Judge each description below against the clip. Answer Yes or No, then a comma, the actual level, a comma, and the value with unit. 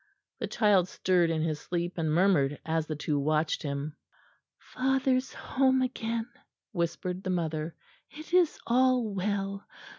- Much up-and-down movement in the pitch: Yes, wide, 6.9 semitones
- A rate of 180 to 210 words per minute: No, average, 140 wpm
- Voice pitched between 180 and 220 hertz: Yes, medium, 185 Hz